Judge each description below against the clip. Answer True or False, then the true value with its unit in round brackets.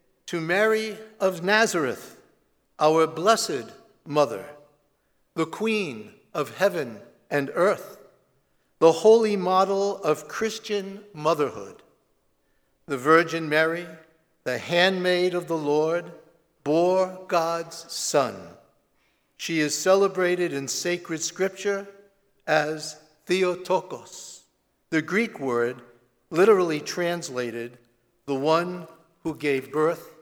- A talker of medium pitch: True (165 Hz)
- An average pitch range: True (3.8 semitones)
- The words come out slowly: True (95 wpm)